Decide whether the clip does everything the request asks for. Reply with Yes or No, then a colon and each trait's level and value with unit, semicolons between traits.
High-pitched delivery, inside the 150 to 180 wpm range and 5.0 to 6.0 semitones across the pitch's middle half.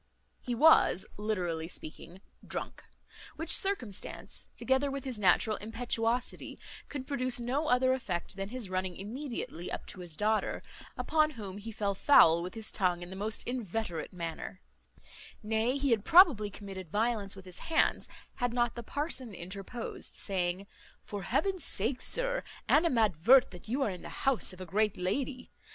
Yes: high, 220 Hz; average, 160 wpm; wide, 5.4 semitones